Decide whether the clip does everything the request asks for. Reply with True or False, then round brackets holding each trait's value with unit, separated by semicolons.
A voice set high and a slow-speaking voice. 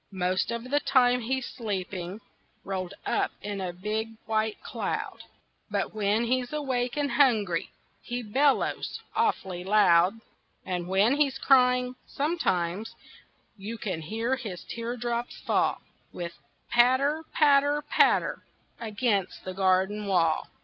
True (225 Hz; 125 wpm)